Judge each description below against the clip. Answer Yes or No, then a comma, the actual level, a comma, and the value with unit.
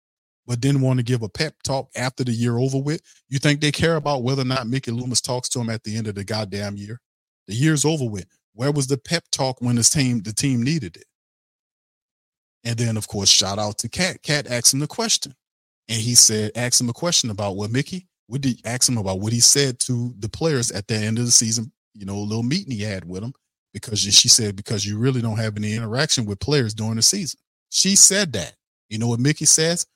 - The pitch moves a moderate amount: Yes, average, 4.2 semitones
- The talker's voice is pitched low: Yes, low, 120 Hz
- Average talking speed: No, fast, 240 wpm